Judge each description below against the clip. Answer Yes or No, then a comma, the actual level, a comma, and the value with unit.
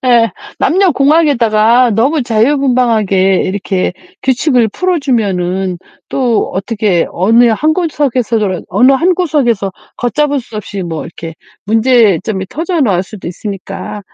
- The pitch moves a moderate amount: No, wide, 5.8 semitones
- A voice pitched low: No, high, 230 Hz